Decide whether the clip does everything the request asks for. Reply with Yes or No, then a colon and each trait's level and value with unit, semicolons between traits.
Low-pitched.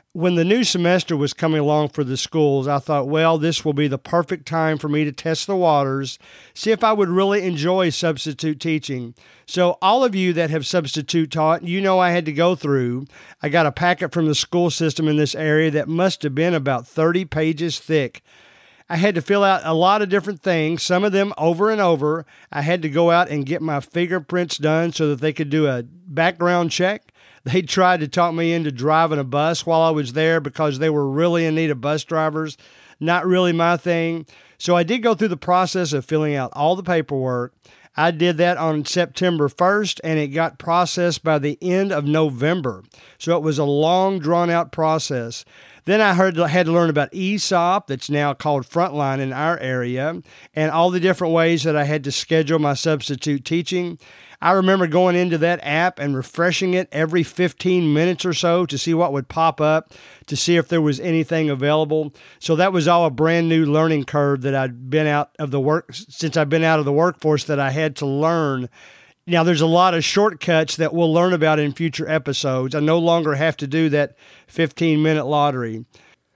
No: medium, 160 Hz